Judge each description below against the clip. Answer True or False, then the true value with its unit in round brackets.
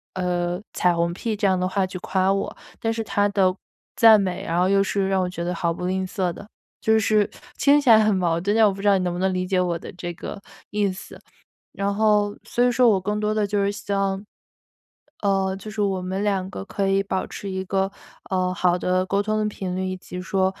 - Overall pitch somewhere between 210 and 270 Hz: False (195 Hz)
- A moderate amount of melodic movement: False (2.0 semitones)